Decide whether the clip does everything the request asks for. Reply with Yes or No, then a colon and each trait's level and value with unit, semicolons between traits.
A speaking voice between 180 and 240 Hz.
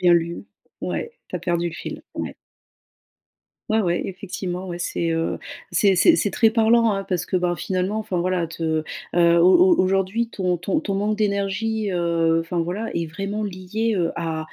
Yes: medium, 185 Hz